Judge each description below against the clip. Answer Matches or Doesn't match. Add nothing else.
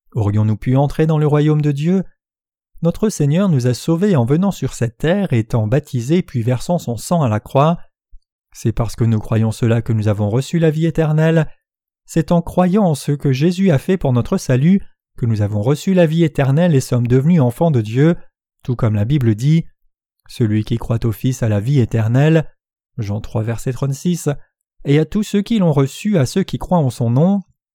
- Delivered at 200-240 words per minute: Matches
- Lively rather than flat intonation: Matches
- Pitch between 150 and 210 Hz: Doesn't match